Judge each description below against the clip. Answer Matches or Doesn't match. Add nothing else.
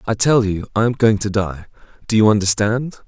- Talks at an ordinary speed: Matches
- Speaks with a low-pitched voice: Matches